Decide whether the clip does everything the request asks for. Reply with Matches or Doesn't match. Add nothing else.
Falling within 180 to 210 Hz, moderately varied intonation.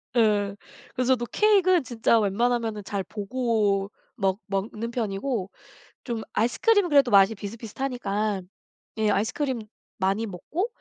Doesn't match